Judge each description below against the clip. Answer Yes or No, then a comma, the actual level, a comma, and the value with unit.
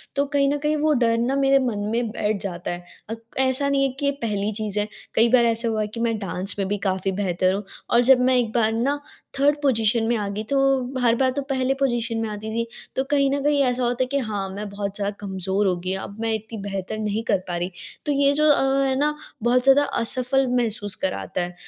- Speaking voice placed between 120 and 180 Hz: No, high, 230 Hz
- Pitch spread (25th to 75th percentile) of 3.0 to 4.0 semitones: No, average, 4.7 semitones